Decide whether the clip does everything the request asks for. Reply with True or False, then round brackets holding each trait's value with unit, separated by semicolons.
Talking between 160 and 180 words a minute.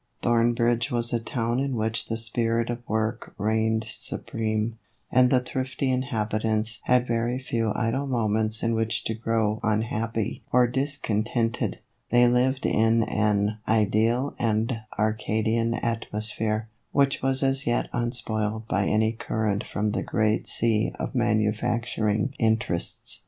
False (135 wpm)